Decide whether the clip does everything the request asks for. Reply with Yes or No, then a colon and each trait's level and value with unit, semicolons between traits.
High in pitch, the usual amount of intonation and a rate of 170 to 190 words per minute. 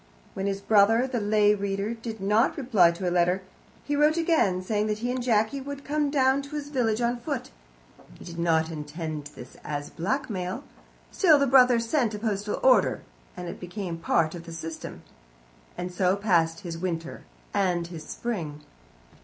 No: high, 205 Hz; wide, 6.2 semitones; average, 180 wpm